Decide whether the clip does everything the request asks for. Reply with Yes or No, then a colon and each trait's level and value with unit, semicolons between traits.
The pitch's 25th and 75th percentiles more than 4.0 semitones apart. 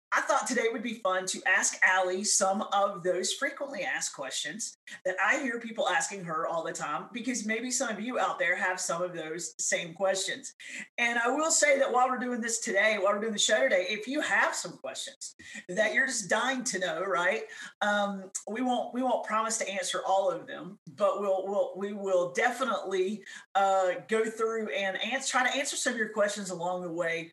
Yes: average, 4.9 semitones